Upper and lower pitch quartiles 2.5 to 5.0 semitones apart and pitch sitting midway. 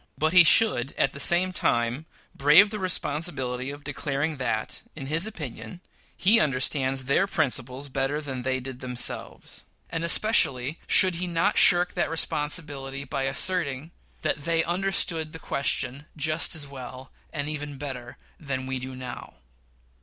Yes: average, 4.0 semitones; medium, 145 Hz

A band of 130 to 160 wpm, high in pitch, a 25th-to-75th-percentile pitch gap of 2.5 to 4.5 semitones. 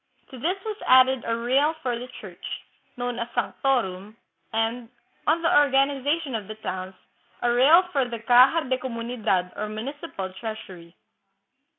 Yes: average, 155 wpm; high, 245 Hz; average, 4.0 semitones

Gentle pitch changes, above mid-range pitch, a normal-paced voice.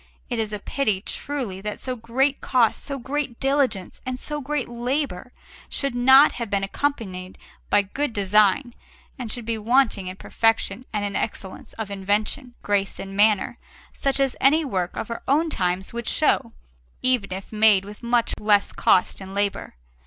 No: average, 4.8 semitones; high, 225 Hz; average, 170 wpm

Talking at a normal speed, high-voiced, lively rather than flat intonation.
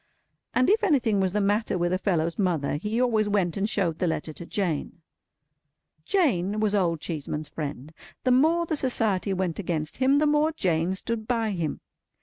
Yes: average, 180 wpm; high, 195 Hz; wide, 6.1 semitones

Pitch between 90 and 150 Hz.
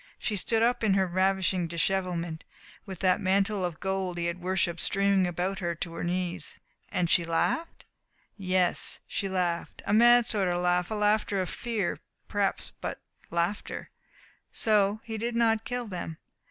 No: high, 190 Hz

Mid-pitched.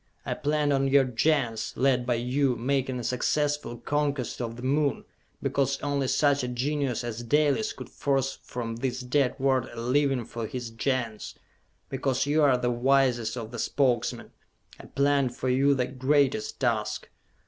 No: low, 130 Hz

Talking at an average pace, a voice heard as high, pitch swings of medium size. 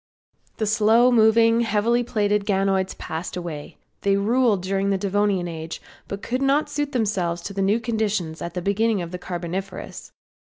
Yes: average, 160 wpm; high, 200 Hz; average, 3.6 semitones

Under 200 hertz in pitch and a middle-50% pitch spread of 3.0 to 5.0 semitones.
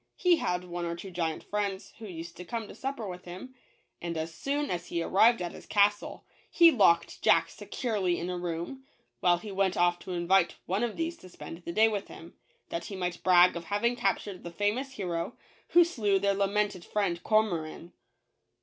Yes: high, 190 Hz; average, 3.7 semitones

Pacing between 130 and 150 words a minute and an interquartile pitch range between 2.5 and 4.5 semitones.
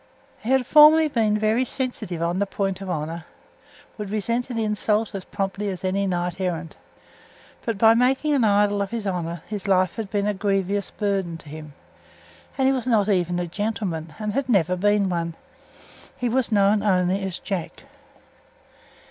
No: average, 175 wpm; average, 3.4 semitones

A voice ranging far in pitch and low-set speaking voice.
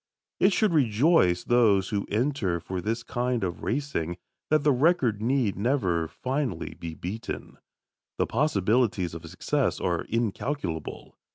Yes: wide, 7.1 semitones; low, 115 Hz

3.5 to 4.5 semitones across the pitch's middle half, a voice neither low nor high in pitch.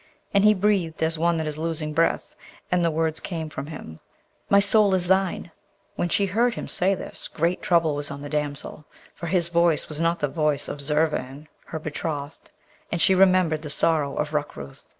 No: average, 3.0 semitones; medium, 160 Hz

